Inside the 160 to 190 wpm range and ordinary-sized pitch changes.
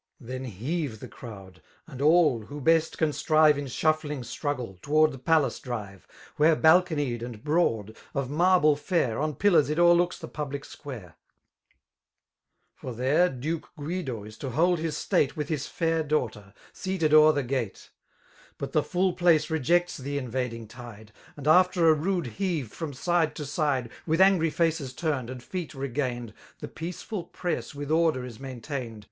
Yes: average, 165 wpm; average, 4.5 semitones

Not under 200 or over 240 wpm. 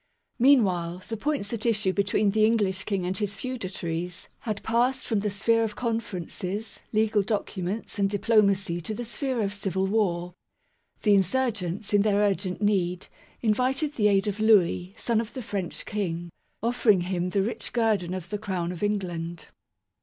No: average, 165 wpm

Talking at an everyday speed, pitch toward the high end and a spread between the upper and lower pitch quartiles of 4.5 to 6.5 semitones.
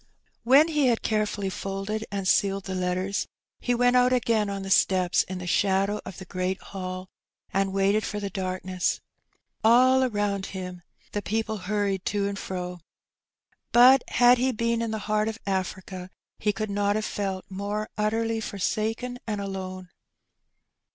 No: average, 160 wpm; high, 200 Hz; average, 2.7 semitones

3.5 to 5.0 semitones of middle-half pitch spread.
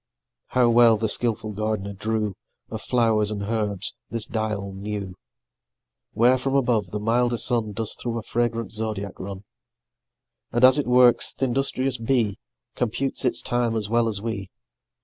No: narrow, 2.4 semitones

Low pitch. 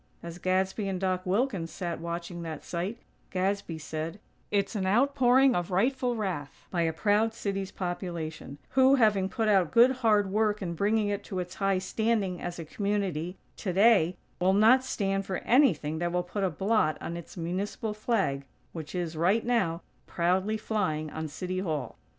No: high, 190 Hz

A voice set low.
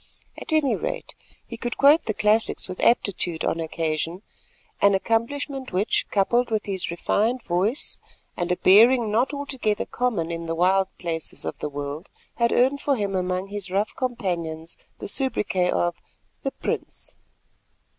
No: high, 205 Hz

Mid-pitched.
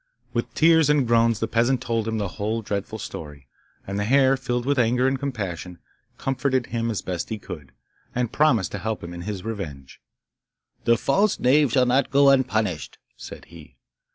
No: low, 115 Hz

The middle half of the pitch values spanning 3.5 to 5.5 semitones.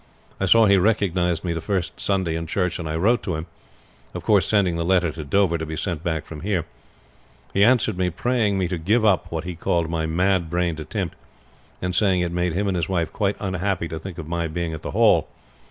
No: average, 2.9 semitones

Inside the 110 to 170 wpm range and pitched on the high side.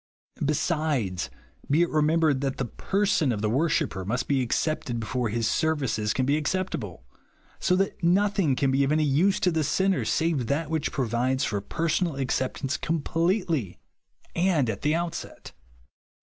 No: average, 160 wpm; medium, 145 Hz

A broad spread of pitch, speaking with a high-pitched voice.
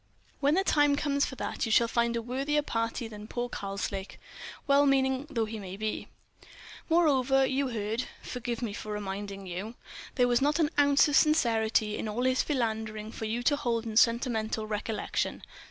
No: average, 4.1 semitones; high, 235 Hz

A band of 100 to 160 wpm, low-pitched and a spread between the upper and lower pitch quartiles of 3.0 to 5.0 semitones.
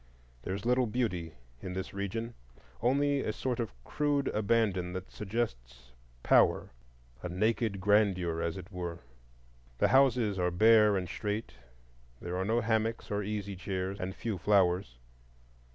Yes: average, 140 wpm; low, 100 Hz; average, 4.0 semitones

